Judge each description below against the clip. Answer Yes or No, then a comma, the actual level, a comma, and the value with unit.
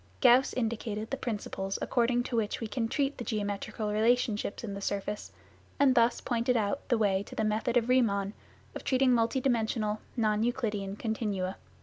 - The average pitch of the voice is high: Yes, high, 225 Hz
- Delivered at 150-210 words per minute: Yes, average, 170 wpm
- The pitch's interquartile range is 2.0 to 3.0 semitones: Yes, average, 2.7 semitones